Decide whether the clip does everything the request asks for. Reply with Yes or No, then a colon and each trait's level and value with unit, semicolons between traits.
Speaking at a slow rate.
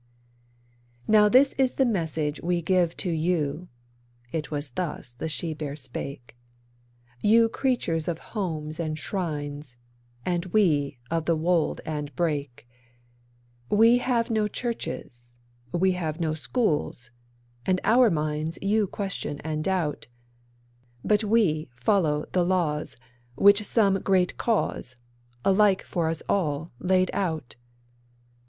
Yes: slow, 125 wpm